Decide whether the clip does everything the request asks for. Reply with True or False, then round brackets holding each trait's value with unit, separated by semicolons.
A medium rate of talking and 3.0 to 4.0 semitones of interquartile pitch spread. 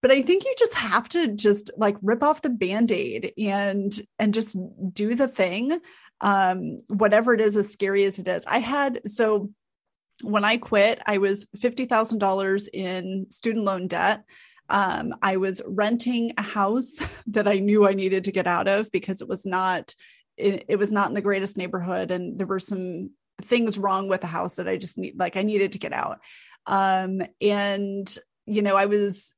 False (190 wpm; 2.6 semitones)